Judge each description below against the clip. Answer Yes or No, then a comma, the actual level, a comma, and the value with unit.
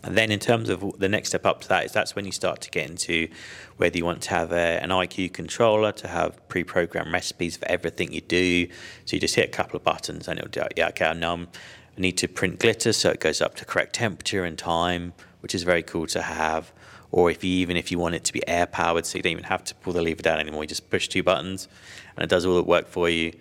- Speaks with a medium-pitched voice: No, very low, 90 Hz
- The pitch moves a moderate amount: No, narrow, 1.8 semitones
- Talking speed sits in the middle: No, fast, 270 wpm